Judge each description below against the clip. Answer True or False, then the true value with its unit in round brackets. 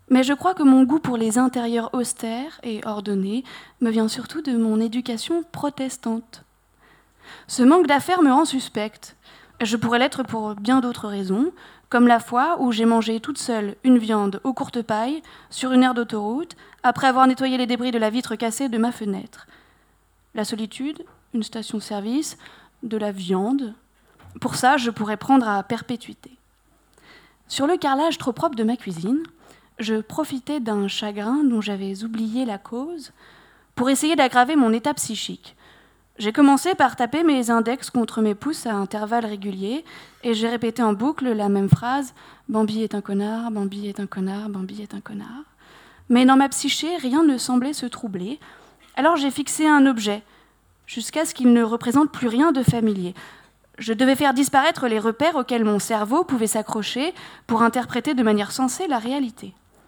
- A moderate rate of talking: True (170 wpm)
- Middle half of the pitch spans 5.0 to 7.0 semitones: False (3.8 semitones)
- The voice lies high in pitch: True (240 Hz)